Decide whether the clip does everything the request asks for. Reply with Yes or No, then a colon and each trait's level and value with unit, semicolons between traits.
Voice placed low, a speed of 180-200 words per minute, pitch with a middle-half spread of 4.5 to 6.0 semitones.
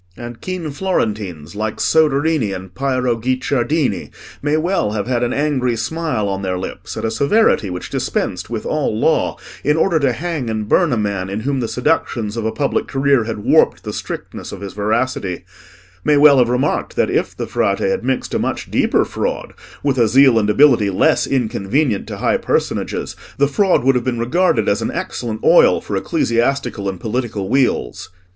Yes: low, 120 Hz; average, 185 wpm; average, 5.0 semitones